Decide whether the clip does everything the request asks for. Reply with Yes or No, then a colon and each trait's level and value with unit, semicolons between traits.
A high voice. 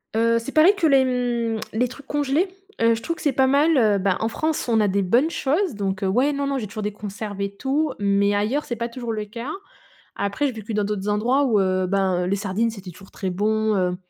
Yes: high, 220 Hz